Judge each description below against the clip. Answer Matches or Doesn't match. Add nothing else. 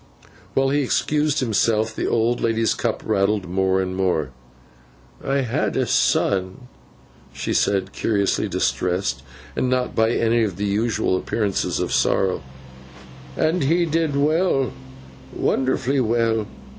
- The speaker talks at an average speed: Doesn't match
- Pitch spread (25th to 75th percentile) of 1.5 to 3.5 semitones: Doesn't match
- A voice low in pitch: Matches